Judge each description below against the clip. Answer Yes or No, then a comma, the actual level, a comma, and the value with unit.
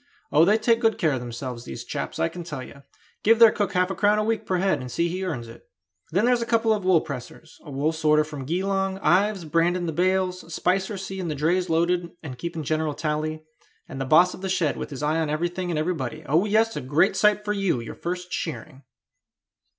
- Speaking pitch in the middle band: Yes, medium, 170 Hz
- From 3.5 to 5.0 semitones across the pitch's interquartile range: Yes, average, 4.0 semitones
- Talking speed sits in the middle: No, fast, 230 wpm